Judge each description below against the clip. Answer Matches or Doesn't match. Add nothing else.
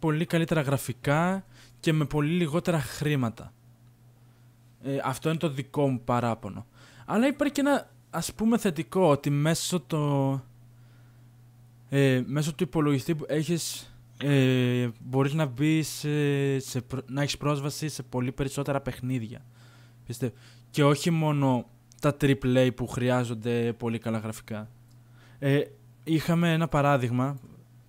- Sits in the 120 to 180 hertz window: Matches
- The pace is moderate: Matches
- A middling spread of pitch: Matches